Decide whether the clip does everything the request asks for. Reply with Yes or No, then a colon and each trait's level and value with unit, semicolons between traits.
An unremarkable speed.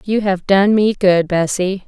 Yes: average, 190 wpm